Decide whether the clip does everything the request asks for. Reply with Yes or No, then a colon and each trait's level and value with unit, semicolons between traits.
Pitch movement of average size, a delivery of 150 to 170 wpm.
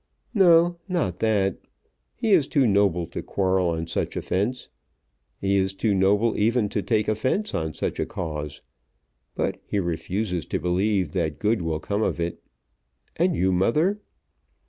Yes: average, 4.7 semitones; average, 155 wpm